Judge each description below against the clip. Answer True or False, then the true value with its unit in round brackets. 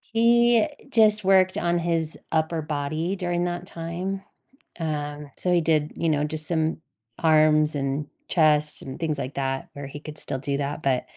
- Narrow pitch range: False (3.0 semitones)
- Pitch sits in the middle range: True (155 Hz)